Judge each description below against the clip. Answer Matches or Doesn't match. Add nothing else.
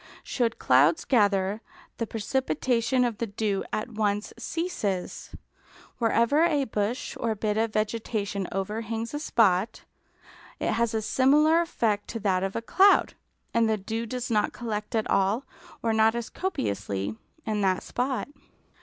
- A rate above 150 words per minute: Doesn't match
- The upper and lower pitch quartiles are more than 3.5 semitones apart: Doesn't match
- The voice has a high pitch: Matches